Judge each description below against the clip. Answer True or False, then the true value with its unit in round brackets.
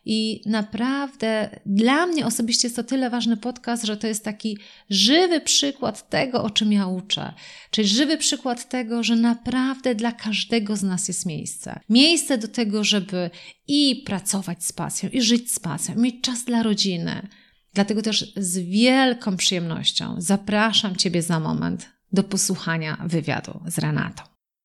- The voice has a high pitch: True (215 Hz)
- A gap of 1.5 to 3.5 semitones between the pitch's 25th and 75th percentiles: False (3.9 semitones)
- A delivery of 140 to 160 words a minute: True (155 wpm)